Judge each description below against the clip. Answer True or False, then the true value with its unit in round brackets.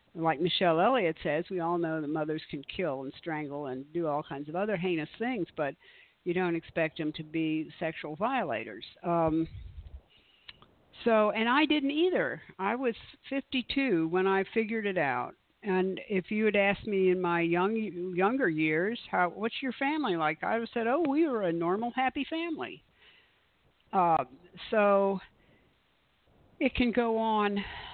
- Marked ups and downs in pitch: True (6.1 semitones)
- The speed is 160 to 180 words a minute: True (165 wpm)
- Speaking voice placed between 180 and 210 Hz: True (185 Hz)